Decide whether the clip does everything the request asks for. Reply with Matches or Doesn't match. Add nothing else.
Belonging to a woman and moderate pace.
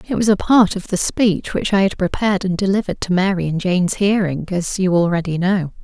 Doesn't match